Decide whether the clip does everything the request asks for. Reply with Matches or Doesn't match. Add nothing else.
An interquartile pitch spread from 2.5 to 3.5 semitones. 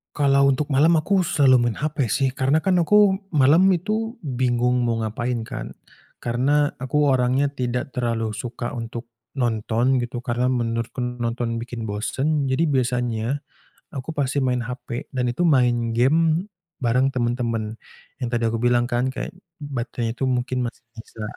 Matches